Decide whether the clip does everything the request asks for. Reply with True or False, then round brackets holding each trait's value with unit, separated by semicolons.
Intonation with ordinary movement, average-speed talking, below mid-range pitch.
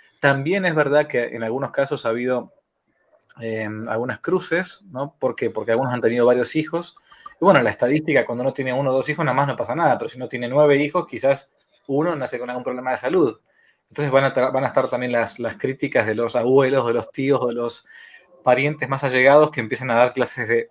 False (3.2 semitones; 230 wpm; 130 Hz)